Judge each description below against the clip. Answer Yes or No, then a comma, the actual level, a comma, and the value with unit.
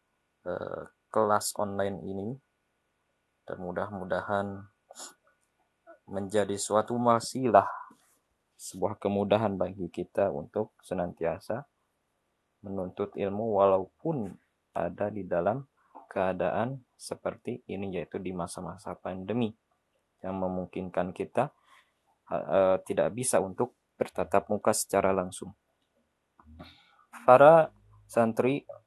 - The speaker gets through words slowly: Yes, slow, 80 wpm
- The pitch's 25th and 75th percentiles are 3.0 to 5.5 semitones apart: No, narrow, 2.5 semitones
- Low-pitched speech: Yes, low, 100 Hz